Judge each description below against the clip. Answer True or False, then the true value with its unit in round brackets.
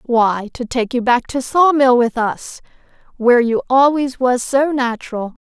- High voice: True (250 Hz)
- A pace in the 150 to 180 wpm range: True (175 wpm)